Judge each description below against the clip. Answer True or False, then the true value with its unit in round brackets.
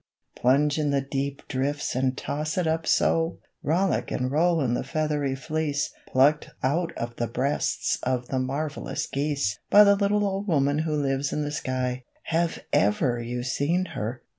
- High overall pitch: False (145 Hz)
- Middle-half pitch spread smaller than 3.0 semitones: False (3.5 semitones)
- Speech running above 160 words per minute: True (170 wpm)